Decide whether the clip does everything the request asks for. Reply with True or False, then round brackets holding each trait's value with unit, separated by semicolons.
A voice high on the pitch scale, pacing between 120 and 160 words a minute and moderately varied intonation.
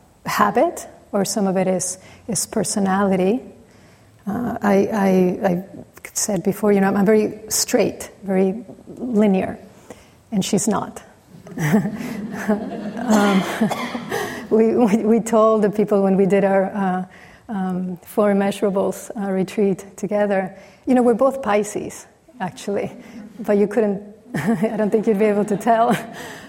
False (205 Hz; 135 wpm; 2.1 semitones)